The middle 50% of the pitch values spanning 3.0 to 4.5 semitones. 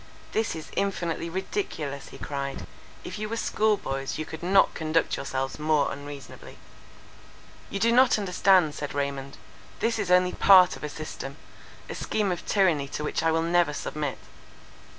No: average, 5.2 semitones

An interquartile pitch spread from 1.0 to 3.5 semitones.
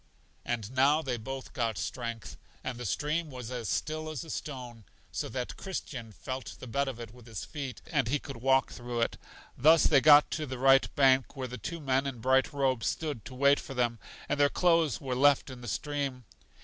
Yes: average, 3.0 semitones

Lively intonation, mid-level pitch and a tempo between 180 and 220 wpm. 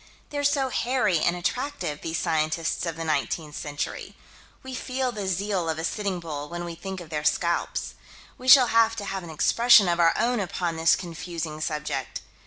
Yes: wide, 5.9 semitones; medium, 175 Hz; average, 190 wpm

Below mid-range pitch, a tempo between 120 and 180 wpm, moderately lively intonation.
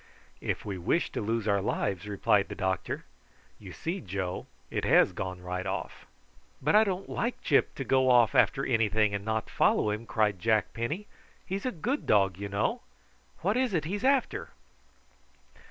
No: low, 110 Hz; average, 175 wpm; wide, 8.4 semitones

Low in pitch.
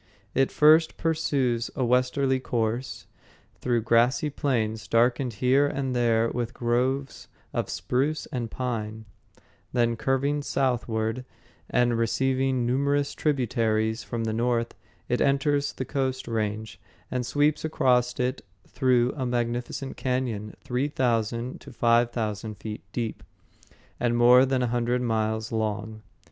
Yes: low, 125 Hz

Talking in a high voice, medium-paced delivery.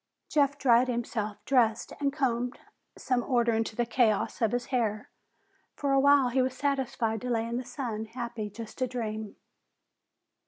Yes: high, 240 Hz; average, 165 wpm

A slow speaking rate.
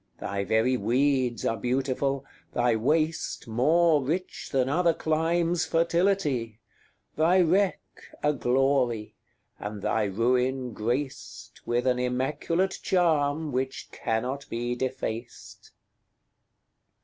Yes: slow, 100 wpm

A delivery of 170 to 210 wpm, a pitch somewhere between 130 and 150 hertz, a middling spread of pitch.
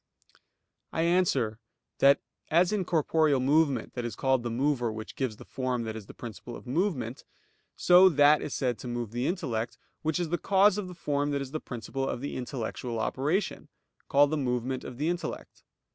Yes: average, 190 wpm; low, 135 Hz; average, 4.8 semitones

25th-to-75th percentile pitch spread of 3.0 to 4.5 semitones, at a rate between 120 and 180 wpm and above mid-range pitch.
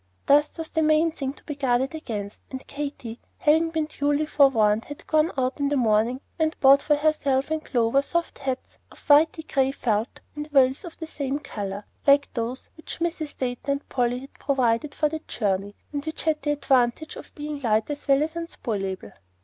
No: average, 3.8 semitones; average, 195 wpm; very high, 280 Hz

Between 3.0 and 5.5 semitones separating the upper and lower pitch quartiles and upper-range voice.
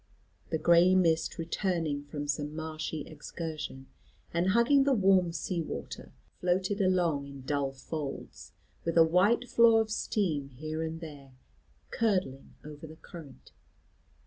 No: average, 4.0 semitones; medium, 165 Hz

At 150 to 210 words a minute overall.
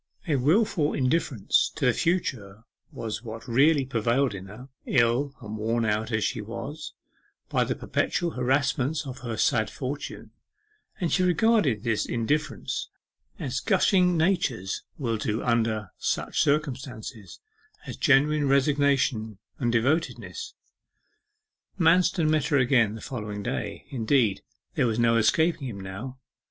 No: slow, 135 wpm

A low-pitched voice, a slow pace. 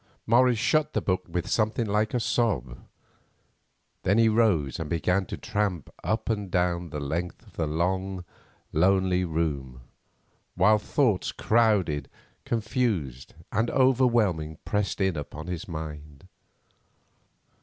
Yes: very low, 95 Hz; slow, 125 wpm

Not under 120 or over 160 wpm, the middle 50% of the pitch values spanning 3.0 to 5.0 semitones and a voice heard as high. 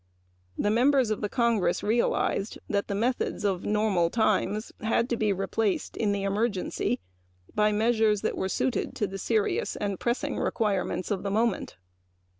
No: average, 155 wpm; narrow, 2.5 semitones; high, 210 Hz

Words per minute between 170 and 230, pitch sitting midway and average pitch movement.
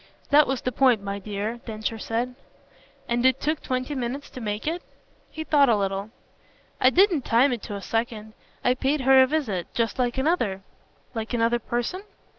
No: average, 185 wpm; high, 240 Hz; average, 3.7 semitones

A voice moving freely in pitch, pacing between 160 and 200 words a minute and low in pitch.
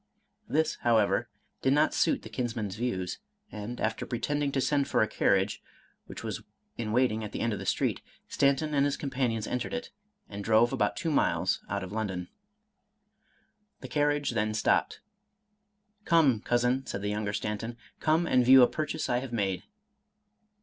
No: average, 4.7 semitones; average, 175 wpm; low, 120 Hz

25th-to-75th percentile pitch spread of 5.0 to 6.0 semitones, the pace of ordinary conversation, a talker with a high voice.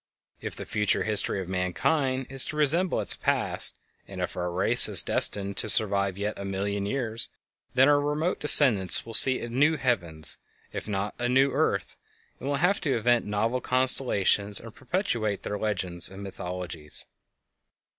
No: average, 5.3 semitones; average, 165 wpm; low, 110 Hz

